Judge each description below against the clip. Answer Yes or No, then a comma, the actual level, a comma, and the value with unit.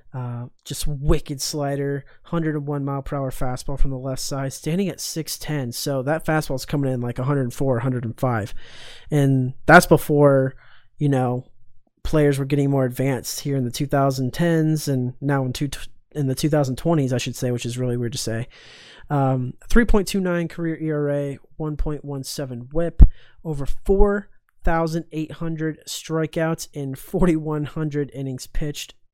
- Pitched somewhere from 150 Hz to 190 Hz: No, medium, 140 Hz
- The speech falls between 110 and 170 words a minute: Yes, average, 140 wpm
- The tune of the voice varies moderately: Yes, average, 3.2 semitones